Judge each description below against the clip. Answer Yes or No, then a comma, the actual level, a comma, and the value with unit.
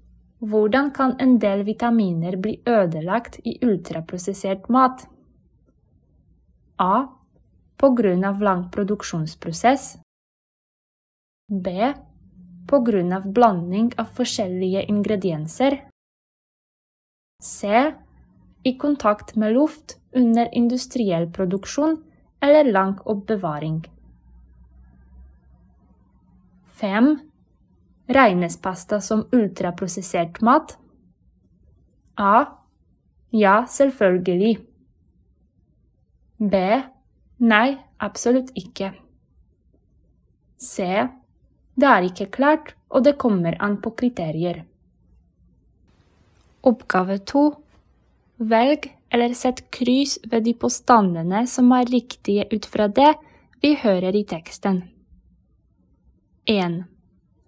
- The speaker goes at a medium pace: No, slow, 80 wpm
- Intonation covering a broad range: No, average, 5.0 semitones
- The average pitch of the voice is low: No, high, 215 Hz